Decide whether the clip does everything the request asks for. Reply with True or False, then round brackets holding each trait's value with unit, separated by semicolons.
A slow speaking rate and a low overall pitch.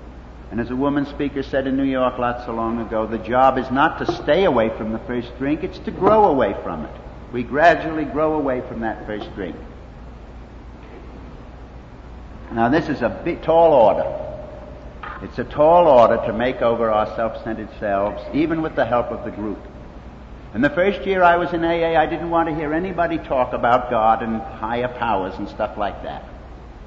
False (190 wpm; 120 Hz)